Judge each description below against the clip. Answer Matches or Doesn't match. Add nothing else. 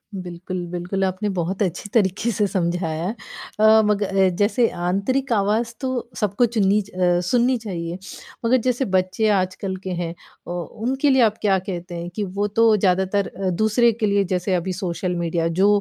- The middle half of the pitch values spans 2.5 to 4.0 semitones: Matches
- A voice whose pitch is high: Matches